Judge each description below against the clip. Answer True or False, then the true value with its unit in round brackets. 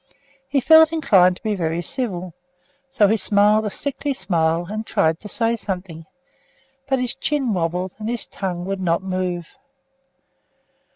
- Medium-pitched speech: False (195 Hz)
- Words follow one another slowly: False (155 wpm)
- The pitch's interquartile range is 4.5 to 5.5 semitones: True (4.9 semitones)